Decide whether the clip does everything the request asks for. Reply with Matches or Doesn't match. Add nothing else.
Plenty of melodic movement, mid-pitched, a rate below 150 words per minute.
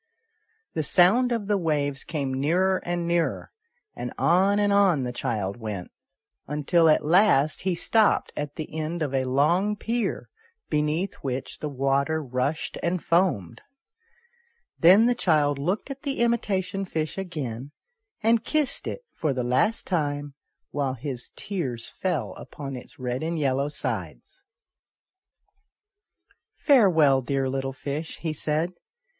Matches